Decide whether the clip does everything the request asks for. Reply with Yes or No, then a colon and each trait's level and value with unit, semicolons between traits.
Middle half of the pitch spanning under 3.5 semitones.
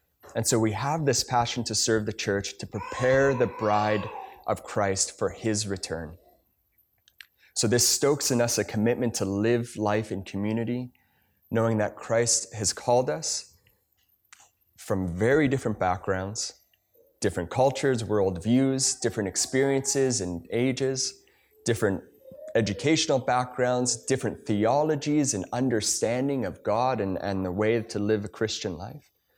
No: average, 4.1 semitones